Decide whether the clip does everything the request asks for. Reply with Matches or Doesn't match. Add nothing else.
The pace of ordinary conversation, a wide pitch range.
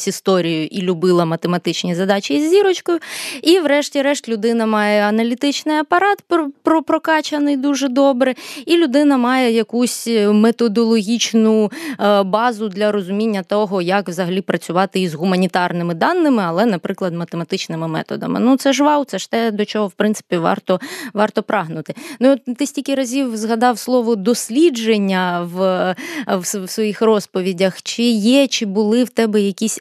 Matches